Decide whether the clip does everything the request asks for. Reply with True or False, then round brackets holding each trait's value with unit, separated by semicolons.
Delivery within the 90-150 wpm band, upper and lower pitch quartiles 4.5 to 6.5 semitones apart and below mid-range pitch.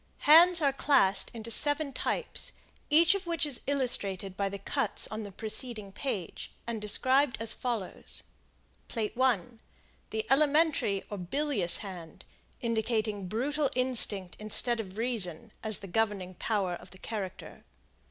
False (140 wpm; 5.4 semitones; 225 Hz)